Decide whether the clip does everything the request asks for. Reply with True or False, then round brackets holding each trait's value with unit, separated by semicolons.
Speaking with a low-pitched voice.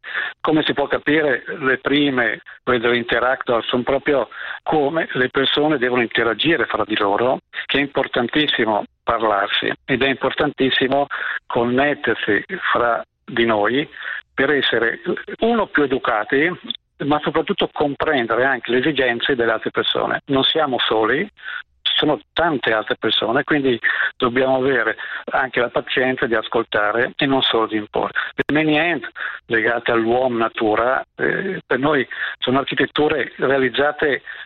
True (130 Hz)